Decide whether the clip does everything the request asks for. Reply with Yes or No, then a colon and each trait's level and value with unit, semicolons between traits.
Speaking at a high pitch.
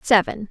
Yes: high, 210 Hz